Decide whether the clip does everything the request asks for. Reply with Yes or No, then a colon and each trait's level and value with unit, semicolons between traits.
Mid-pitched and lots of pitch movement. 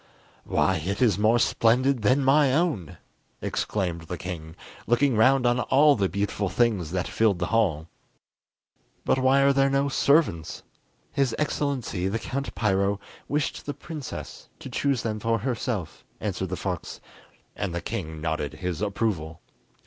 No: low, 110 Hz; wide, 6.7 semitones